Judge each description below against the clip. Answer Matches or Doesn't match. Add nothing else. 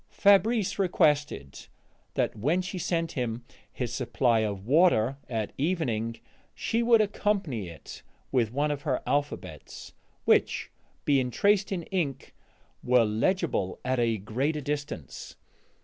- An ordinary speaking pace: Doesn't match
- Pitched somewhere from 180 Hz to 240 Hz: Doesn't match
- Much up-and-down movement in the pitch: Matches